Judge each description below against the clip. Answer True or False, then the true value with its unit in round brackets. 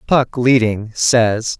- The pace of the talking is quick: False (115 wpm)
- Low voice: True (115 Hz)